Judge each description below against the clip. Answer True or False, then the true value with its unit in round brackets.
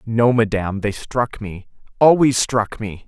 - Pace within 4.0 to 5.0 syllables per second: True (4.1 syllables/s)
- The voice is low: True (110 Hz)